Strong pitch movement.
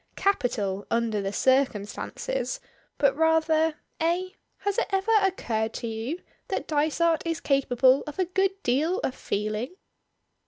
Yes: wide, 7.5 semitones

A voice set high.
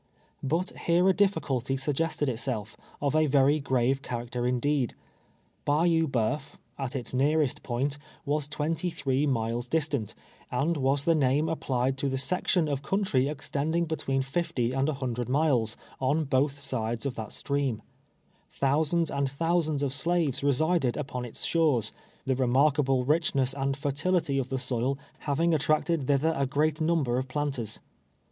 No: medium, 140 Hz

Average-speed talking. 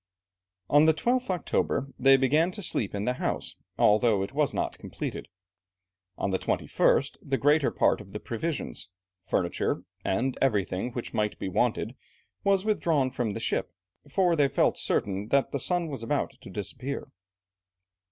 Yes: average, 160 wpm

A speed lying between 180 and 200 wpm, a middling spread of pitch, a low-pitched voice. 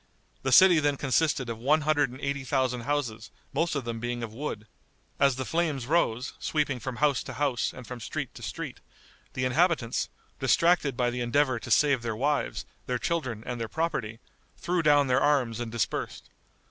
Yes: average, 185 wpm; average, 3.6 semitones; low, 130 Hz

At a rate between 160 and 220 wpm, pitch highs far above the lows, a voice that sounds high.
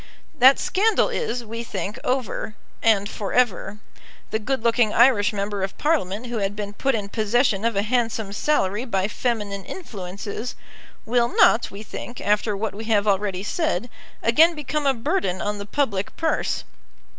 No: average, 165 wpm; average, 3.7 semitones; high, 220 Hz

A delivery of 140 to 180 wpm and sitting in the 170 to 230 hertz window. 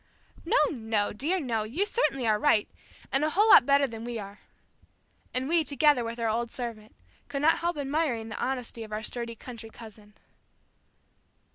No: average, 175 wpm; high, 240 Hz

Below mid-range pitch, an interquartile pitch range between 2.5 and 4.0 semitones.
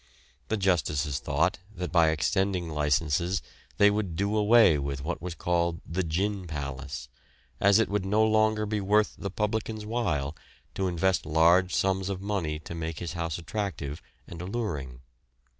No: very low, 90 Hz; average, 4.5 semitones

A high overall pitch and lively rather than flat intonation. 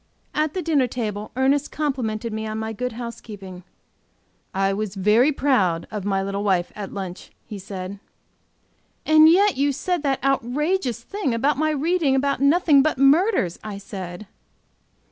Yes: high, 245 Hz; wide, 6.4 semitones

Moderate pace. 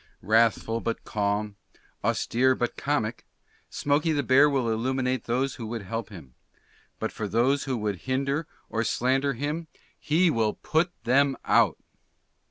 Yes: average, 145 wpm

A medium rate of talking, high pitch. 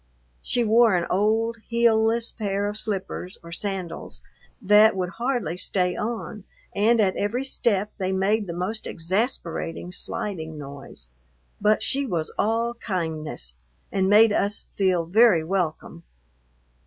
No: slow, 130 wpm; high, 200 Hz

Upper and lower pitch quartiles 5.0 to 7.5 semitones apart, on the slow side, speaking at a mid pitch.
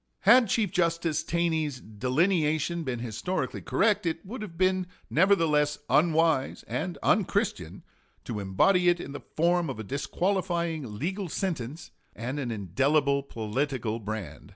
Yes: wide, 5.6 semitones; slow, 130 wpm; medium, 160 Hz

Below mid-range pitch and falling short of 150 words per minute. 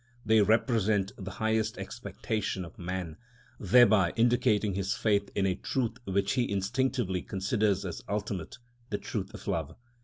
Yes: low, 105 Hz; average, 140 wpm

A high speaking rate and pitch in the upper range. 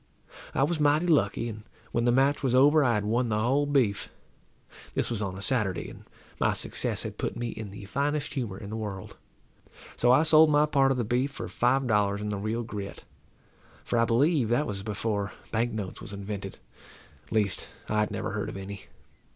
No: fast, 210 wpm; low, 115 Hz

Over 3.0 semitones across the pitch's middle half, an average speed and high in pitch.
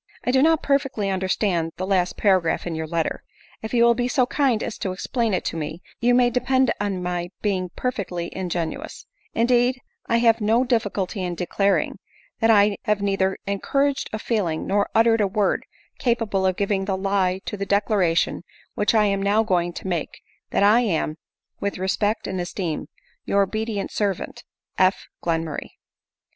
Yes: average, 3.7 semitones; average, 185 wpm; high, 200 Hz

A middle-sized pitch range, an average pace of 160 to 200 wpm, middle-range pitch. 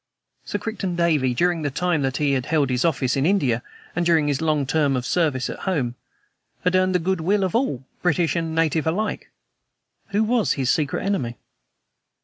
Yes: average, 4.7 semitones; average, 185 wpm; medium, 160 Hz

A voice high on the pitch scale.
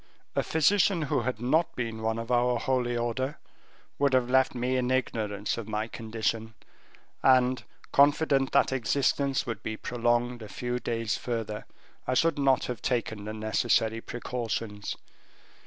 No: low, 120 Hz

